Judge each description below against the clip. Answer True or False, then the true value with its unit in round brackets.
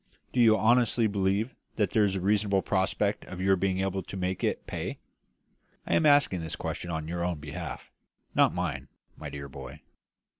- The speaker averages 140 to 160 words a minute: False (185 wpm)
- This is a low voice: True (95 Hz)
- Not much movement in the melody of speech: False (3.4 semitones)